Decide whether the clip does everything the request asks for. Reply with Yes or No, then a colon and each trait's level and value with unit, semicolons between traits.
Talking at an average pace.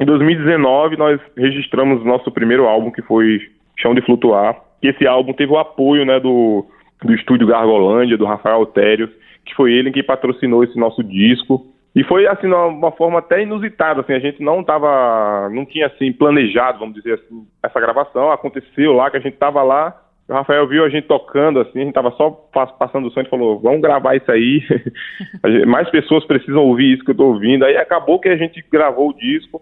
No: fast, 205 wpm